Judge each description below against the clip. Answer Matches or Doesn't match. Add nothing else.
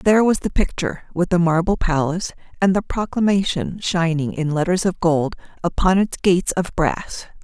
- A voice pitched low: Doesn't match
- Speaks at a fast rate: Doesn't match